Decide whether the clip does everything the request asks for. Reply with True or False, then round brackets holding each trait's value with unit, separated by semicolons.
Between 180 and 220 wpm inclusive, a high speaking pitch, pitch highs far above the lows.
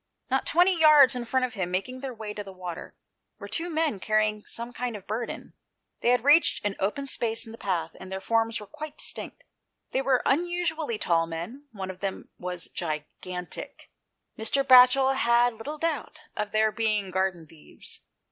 True (185 wpm; 225 Hz; 5.9 semitones)